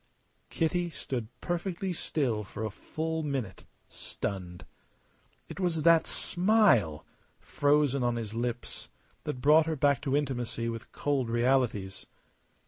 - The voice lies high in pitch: No, low, 135 Hz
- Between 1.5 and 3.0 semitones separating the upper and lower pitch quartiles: No, wide, 5.6 semitones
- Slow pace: Yes, slow, 125 wpm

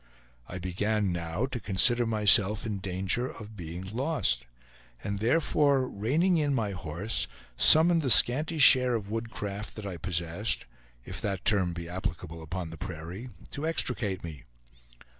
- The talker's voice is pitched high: No, low, 105 Hz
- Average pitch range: No, wide, 5.7 semitones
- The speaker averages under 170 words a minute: Yes, average, 145 wpm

